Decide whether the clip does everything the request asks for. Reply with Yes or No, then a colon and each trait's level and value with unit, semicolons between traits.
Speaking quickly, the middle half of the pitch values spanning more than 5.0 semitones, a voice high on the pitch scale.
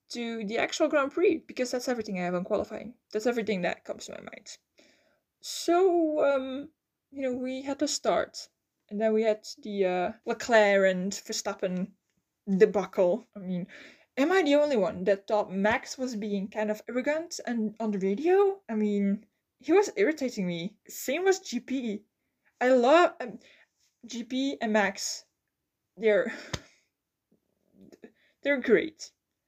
No: average, 150 wpm; wide, 5.4 semitones; high, 230 Hz